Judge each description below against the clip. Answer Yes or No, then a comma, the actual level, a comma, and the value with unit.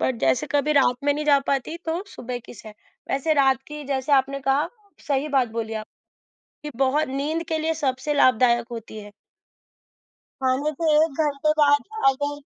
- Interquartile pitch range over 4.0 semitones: No, narrow, 2.6 semitones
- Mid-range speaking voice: No, very high, 275 Hz